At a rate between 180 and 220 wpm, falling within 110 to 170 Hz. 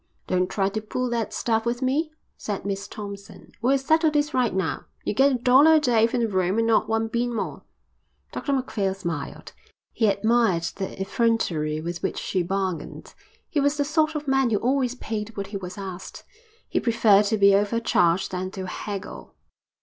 No: average, 190 wpm; high, 220 Hz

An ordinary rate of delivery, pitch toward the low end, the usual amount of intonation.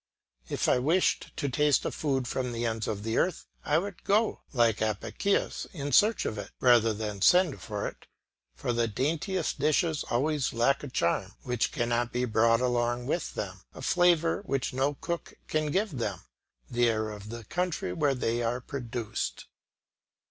Yes: average, 175 wpm; low, 125 Hz; average, 5.0 semitones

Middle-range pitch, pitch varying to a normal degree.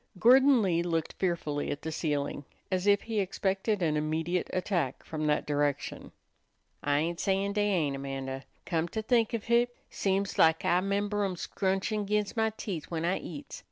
Yes: medium, 180 Hz; average, 4.7 semitones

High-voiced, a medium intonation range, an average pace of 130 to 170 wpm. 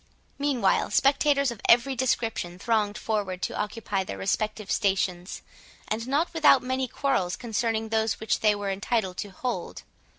Yes: high, 220 Hz; average, 4.3 semitones; average, 145 wpm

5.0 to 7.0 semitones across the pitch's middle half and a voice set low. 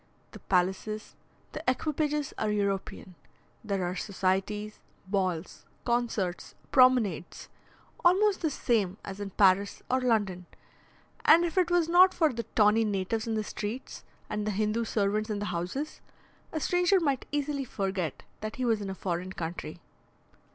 No: wide, 5.6 semitones; high, 215 Hz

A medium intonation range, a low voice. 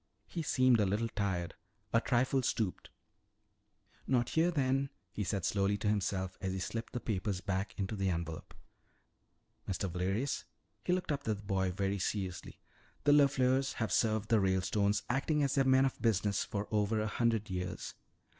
Yes: average, 5.0 semitones; low, 105 Hz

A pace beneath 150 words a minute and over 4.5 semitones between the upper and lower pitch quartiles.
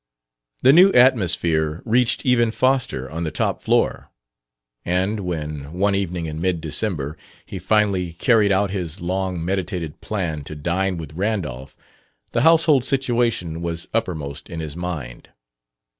Yes: average, 140 wpm; average, 5.3 semitones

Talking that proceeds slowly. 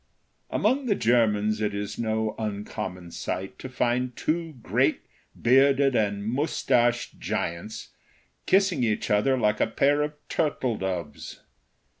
Yes: slow, 125 wpm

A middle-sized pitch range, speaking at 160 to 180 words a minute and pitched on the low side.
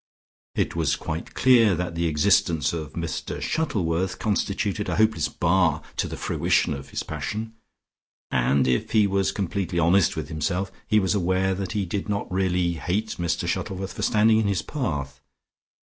Yes: average, 3.7 semitones; average, 165 wpm; very low, 95 Hz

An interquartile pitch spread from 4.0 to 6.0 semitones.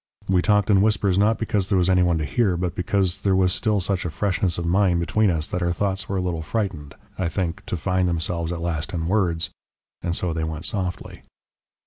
No: narrow, 2.5 semitones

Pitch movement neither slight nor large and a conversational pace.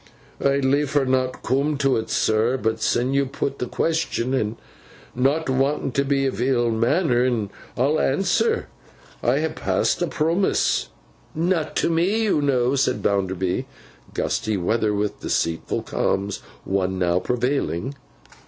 No: average, 4.4 semitones; slow, 130 wpm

